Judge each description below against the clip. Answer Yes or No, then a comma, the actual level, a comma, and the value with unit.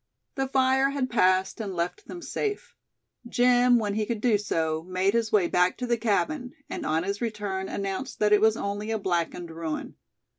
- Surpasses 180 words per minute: Yes, average, 190 wpm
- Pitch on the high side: Yes, high, 210 Hz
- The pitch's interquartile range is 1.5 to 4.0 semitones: No, average, 4.7 semitones